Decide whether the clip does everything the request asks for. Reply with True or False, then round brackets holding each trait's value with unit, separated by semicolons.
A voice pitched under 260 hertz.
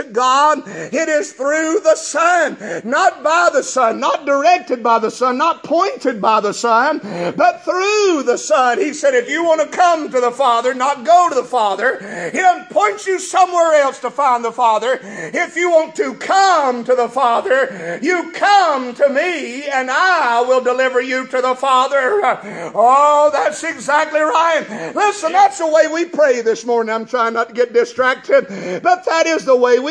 False (300 Hz)